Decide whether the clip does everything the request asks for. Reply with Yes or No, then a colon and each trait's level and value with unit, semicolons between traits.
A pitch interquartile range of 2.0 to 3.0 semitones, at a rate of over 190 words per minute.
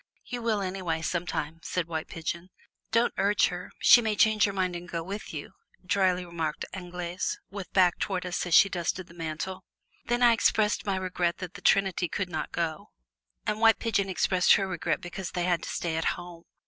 Yes: narrow, 2.6 semitones; average, 200 wpm